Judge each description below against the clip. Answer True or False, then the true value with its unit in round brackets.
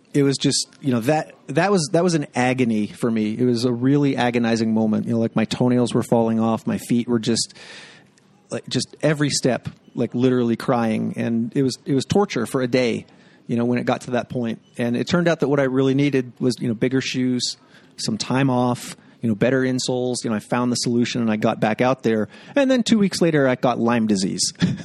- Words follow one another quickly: True (235 wpm)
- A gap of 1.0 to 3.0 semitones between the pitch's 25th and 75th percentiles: True (2.7 semitones)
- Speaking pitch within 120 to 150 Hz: True (125 Hz)